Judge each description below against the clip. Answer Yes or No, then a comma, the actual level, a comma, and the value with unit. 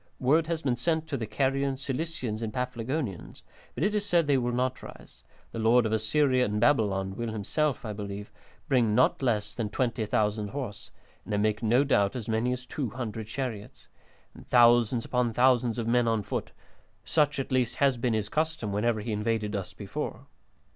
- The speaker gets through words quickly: No, average, 185 wpm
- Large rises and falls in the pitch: No, average, 3.6 semitones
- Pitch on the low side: Yes, low, 120 Hz